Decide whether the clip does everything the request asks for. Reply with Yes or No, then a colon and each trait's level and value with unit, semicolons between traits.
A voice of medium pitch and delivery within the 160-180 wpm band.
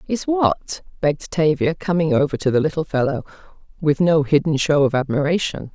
Yes: medium, 155 Hz; average, 165 wpm